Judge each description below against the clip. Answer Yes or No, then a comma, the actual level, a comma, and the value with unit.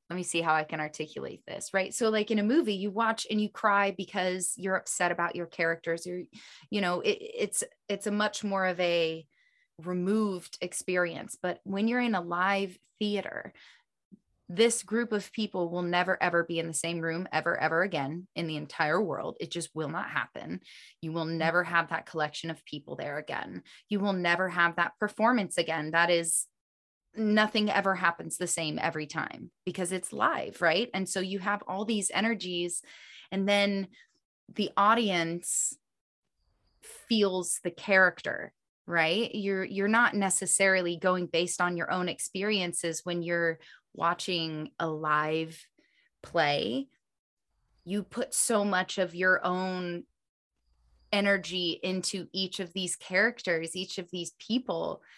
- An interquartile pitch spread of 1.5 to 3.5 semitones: Yes, average, 3.1 semitones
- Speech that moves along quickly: No, average, 160 wpm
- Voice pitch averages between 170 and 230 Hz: Yes, medium, 185 Hz